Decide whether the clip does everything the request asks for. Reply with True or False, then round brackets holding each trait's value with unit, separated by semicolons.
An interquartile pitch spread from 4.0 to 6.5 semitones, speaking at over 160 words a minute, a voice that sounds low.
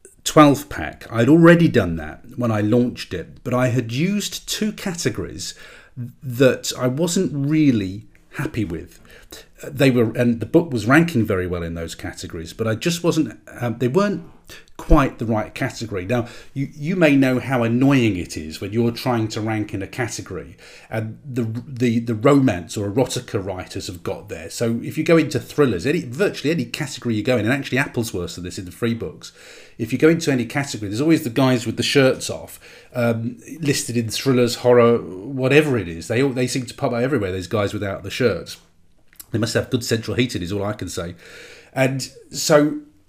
True (4.4 semitones; 200 wpm; 120 Hz)